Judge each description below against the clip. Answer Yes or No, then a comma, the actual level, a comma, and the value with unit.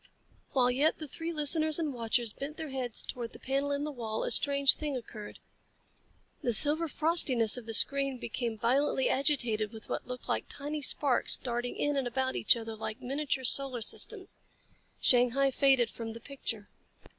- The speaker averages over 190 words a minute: No, average, 175 wpm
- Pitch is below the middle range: No, very high, 260 Hz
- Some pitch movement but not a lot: Yes, average, 3.3 semitones